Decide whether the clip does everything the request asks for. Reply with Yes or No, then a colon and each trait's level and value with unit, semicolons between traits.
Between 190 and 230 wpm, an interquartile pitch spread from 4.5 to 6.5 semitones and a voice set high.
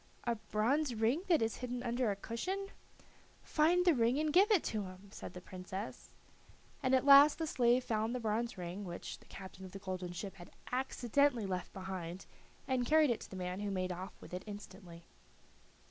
Yes: average, 195 wpm; wide, 5.6 semitones; high, 225 Hz